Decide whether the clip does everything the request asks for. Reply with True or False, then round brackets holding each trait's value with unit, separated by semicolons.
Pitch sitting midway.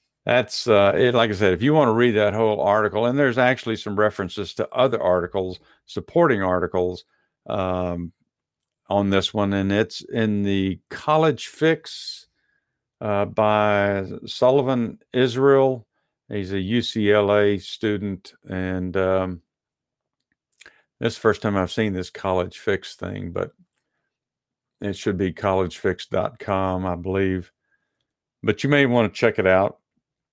False (100 Hz)